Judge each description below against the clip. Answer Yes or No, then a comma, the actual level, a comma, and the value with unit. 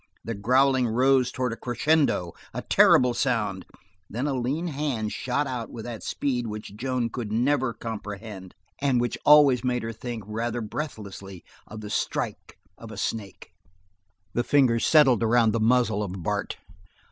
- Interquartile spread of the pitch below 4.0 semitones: Yes, average, 3.2 semitones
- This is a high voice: No, low, 120 Hz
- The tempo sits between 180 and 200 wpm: No, average, 160 wpm